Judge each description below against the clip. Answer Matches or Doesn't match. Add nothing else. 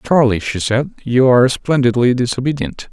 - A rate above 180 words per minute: Doesn't match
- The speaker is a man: Matches